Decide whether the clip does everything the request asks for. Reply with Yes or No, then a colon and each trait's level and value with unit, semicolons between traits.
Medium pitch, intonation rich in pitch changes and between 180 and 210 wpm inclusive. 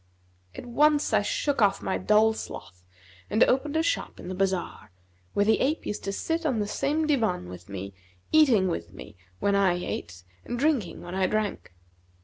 No: high, 210 Hz; wide, 7.9 semitones; average, 185 wpm